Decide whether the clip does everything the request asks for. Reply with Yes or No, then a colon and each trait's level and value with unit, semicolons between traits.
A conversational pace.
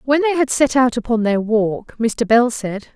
No: fast, 225 wpm